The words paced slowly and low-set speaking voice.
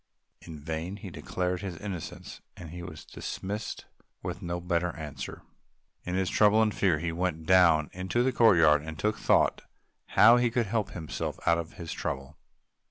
No: average, 165 wpm; very low, 90 Hz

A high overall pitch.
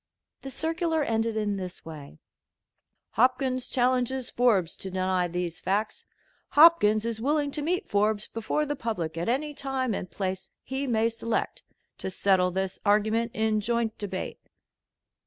Yes: high, 225 Hz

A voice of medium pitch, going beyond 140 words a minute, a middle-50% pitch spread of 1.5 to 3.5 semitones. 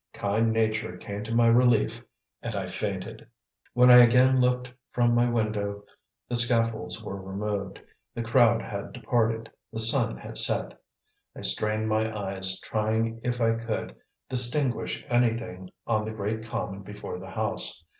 No: low, 110 Hz; average, 150 wpm; narrow, 2.6 semitones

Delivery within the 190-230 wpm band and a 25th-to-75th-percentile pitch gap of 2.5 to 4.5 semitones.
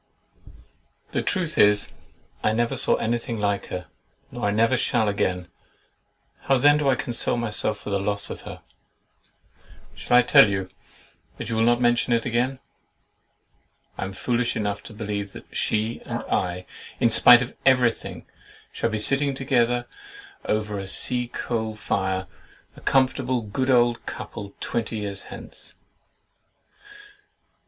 No: average, 145 wpm; average, 3.2 semitones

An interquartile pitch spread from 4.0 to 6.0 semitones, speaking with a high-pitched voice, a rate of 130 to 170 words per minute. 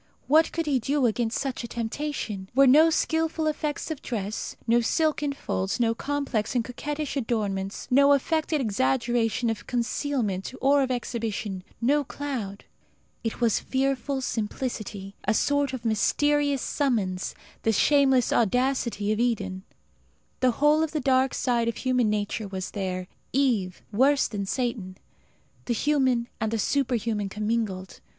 Yes: average, 4.7 semitones; high, 240 Hz; average, 145 wpm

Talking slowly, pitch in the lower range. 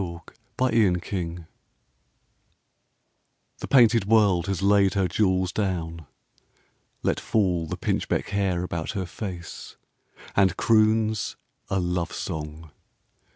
Yes: slow, 110 wpm; very low, 95 Hz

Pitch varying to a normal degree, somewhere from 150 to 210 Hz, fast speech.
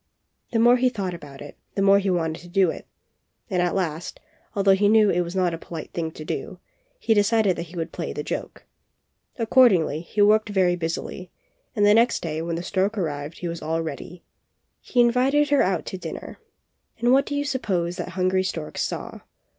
Yes: average, 4.4 semitones; medium, 185 Hz; fast, 210 wpm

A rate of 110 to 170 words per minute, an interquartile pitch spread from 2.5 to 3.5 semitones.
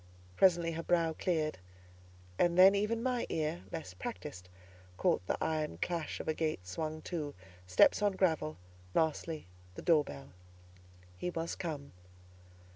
Yes: average, 140 wpm; average, 3.2 semitones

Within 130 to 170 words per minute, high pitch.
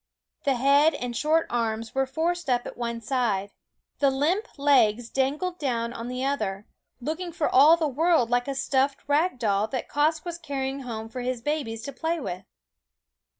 No: average, 180 wpm; very high, 270 Hz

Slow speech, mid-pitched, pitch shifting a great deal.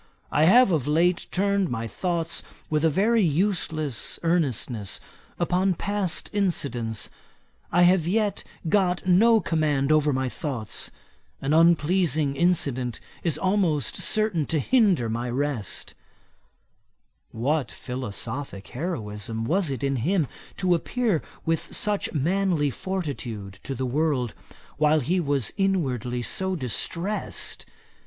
Yes: slow, 120 wpm; medium, 155 Hz; wide, 6.1 semitones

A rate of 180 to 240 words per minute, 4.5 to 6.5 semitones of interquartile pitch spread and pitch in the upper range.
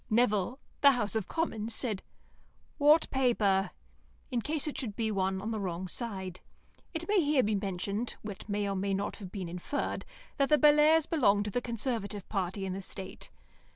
Yes: average, 185 wpm; average, 5.3 semitones; high, 215 Hz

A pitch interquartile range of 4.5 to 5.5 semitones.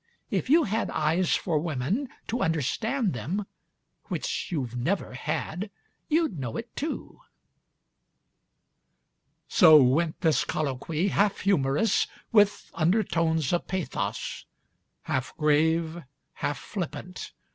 Yes: average, 5.2 semitones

